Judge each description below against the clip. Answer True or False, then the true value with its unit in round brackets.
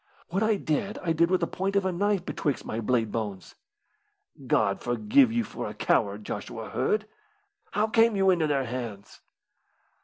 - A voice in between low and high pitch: True (180 Hz)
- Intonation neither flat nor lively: False (8.7 semitones)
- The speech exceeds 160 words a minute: True (175 wpm)